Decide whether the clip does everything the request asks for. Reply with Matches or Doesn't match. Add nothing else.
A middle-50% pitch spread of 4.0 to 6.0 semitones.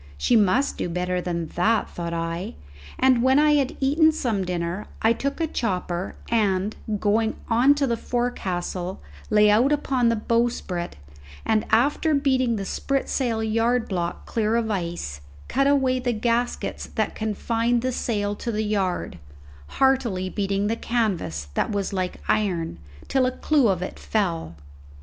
Matches